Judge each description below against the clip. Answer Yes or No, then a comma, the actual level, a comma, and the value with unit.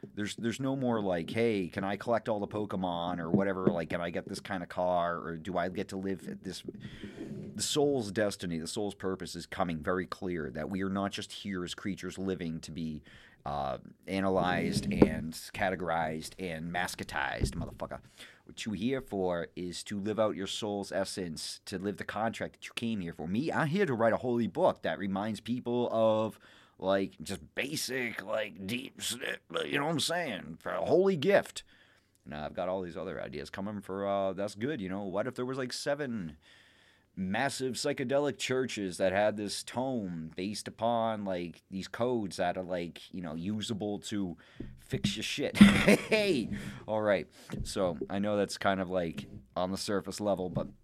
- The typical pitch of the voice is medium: No, low, 100 Hz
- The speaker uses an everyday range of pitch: Yes, average, 3.4 semitones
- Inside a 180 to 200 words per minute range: Yes, average, 190 wpm